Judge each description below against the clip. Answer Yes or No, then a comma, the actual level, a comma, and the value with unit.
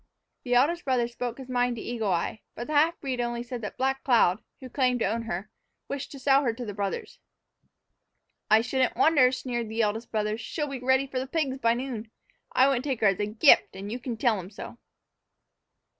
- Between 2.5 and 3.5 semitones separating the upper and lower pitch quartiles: Yes, average, 3.0 semitones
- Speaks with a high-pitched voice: Yes, high, 245 Hz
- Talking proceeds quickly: Yes, fast, 220 wpm